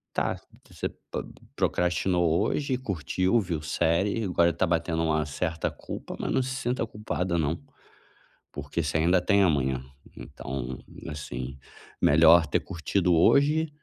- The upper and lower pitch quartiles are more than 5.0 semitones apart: No, average, 4.0 semitones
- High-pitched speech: No, very low, 85 Hz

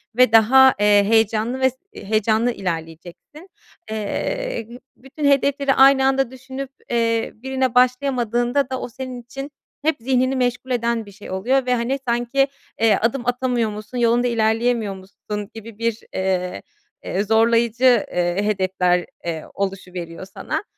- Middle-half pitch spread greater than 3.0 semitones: Yes, average, 3.8 semitones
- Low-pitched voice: No, high, 235 Hz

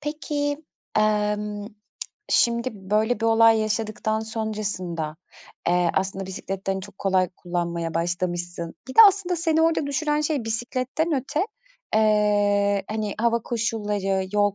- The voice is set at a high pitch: Yes, high, 210 Hz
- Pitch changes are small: No, average, 3.8 semitones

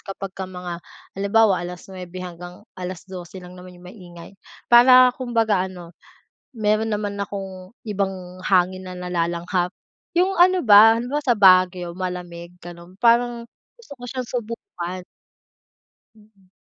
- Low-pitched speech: No, medium, 185 Hz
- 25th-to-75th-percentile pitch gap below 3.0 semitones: No, average, 3.6 semitones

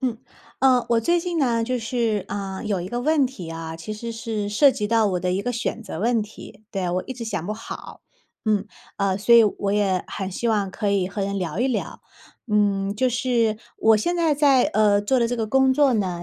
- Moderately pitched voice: No, high, 215 Hz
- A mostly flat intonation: No, average, 3.7 semitones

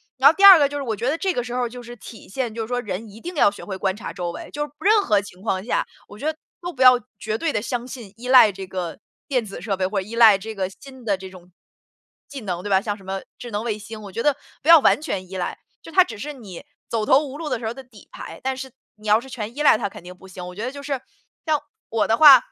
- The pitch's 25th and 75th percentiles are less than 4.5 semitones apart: No, average, 5.1 semitones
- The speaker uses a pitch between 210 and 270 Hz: Yes, high, 230 Hz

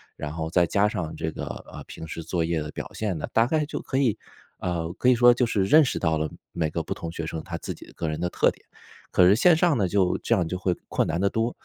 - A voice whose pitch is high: No, very low, 90 Hz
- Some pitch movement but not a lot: No, wide, 5.9 semitones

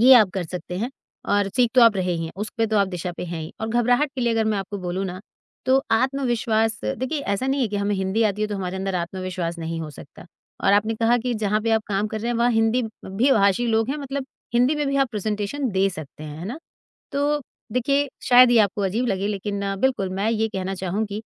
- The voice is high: Yes, high, 215 Hz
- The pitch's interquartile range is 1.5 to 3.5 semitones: No, average, 4.2 semitones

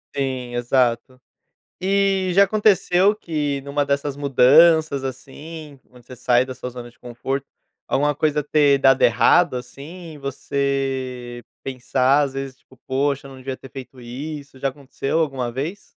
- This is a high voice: No, low, 135 Hz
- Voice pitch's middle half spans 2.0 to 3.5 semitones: Yes, narrow, 2.6 semitones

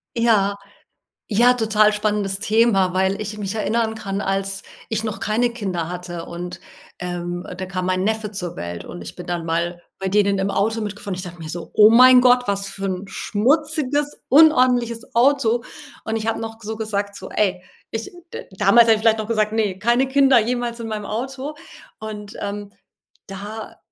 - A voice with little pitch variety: No, average, 3.1 semitones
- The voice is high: Yes, high, 210 Hz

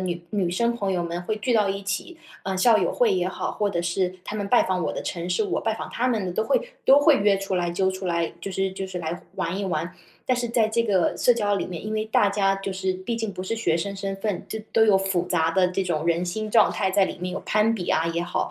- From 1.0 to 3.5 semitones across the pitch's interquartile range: Yes, average, 3.1 semitones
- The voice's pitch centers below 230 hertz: Yes, high, 195 Hz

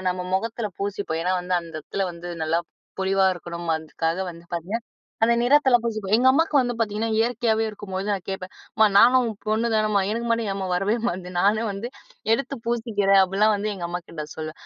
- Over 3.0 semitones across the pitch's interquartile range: Yes, average, 4.0 semitones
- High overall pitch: Yes, high, 205 Hz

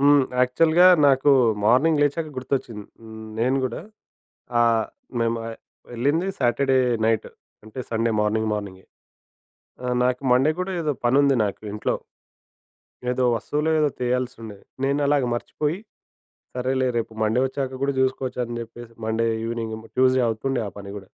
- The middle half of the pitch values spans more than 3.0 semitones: Yes, average, 3.4 semitones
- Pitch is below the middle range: Yes, low, 125 Hz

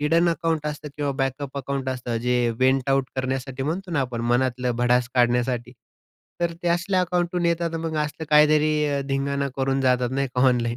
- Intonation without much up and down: No, average, 3.4 semitones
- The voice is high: No, low, 135 Hz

